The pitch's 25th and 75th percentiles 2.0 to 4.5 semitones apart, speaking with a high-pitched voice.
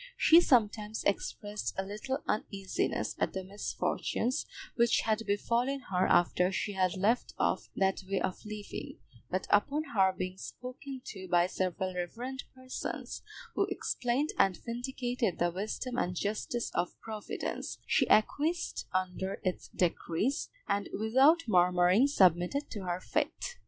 No: average, 5.0 semitones; high, 210 Hz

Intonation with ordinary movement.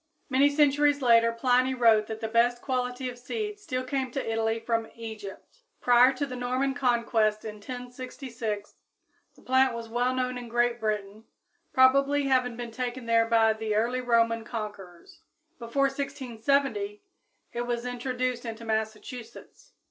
No: narrow, 2.3 semitones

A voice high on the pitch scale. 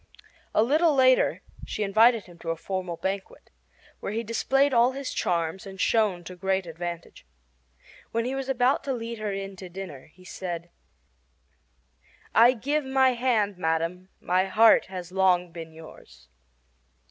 Yes: high, 195 Hz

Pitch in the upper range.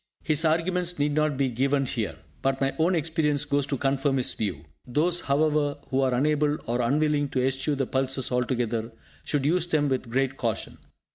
No: medium, 140 Hz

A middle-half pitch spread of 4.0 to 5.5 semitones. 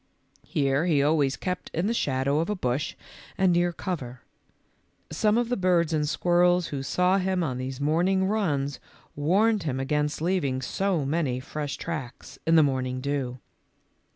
Yes: average, 4.9 semitones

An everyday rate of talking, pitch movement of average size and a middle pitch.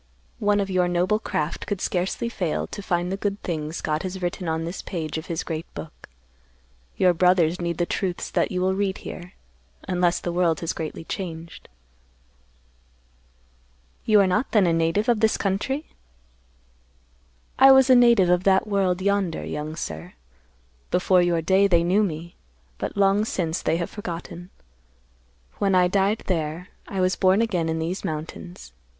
Yes: average, 170 wpm; average, 3.0 semitones; medium, 180 Hz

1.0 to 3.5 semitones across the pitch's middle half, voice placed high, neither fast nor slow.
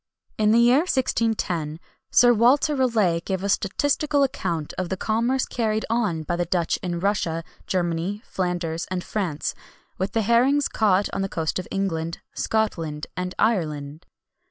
No: average, 5.3 semitones; high, 195 Hz; average, 155 wpm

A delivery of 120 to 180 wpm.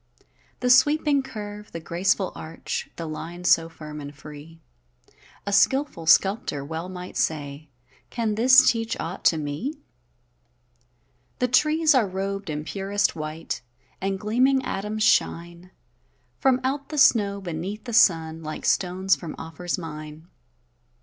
Yes: slow, 135 wpm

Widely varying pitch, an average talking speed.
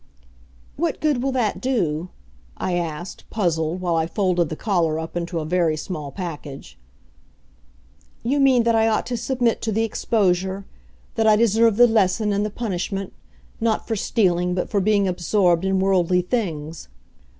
No: average, 4.4 semitones; average, 160 wpm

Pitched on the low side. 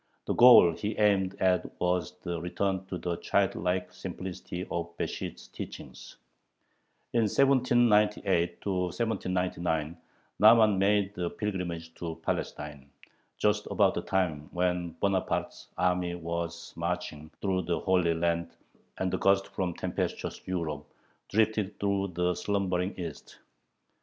Yes: very low, 90 Hz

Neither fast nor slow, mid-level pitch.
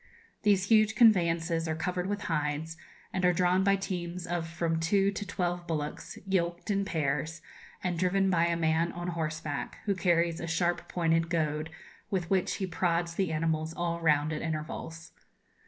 Yes: average, 170 wpm; medium, 170 Hz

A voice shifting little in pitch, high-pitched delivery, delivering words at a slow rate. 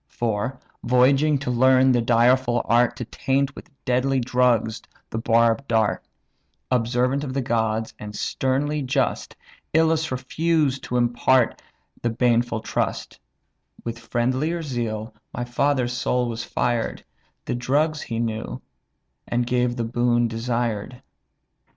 No: narrow, 2.1 semitones; low, 125 Hz; slow, 125 wpm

